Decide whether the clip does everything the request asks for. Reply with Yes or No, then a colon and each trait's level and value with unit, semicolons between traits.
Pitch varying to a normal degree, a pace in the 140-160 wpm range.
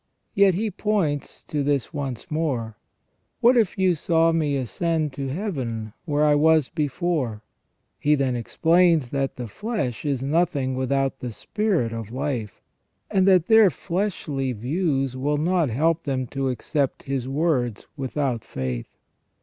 Yes: average, 4.5 semitones; average, 150 wpm